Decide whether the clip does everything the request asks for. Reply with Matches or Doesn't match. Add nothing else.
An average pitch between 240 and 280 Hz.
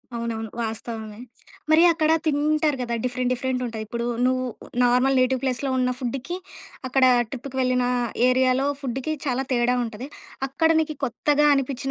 Matches